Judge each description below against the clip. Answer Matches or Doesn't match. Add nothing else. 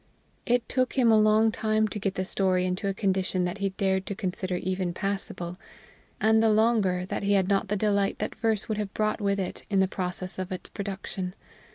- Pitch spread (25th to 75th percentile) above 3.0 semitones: Doesn't match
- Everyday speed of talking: Doesn't match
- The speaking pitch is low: Doesn't match